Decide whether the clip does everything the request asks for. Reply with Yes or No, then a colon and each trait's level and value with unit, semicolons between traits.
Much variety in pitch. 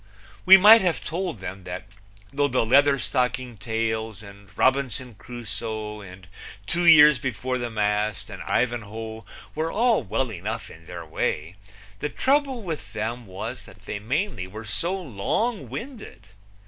Yes: wide, 6.3 semitones